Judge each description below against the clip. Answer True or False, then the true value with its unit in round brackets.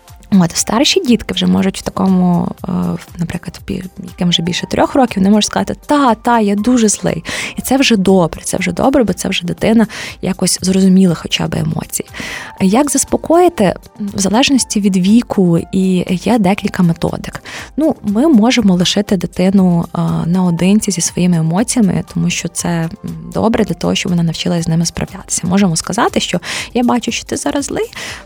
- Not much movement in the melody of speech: False (4.0 semitones)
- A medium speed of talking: False (165 wpm)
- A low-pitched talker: False (195 Hz)